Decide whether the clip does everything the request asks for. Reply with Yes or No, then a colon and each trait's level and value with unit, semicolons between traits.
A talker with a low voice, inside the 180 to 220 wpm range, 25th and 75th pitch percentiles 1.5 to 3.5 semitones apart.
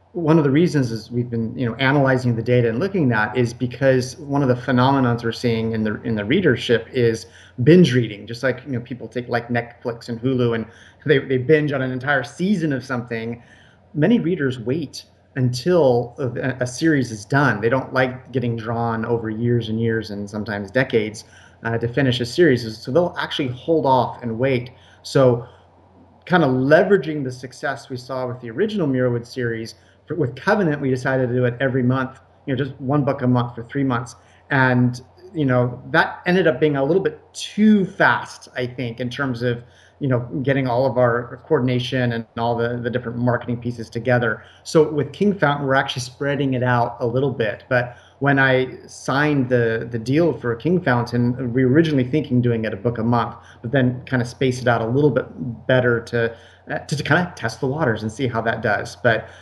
Yes: low, 125 Hz; fast, 205 wpm; narrow, 2.6 semitones